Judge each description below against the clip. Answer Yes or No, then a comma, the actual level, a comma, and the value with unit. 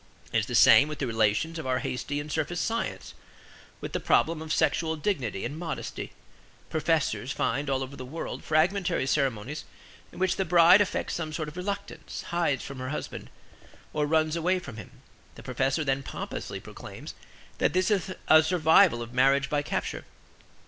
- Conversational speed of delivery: Yes, average, 175 wpm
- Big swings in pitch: No, average, 4.1 semitones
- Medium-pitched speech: Yes, medium, 155 Hz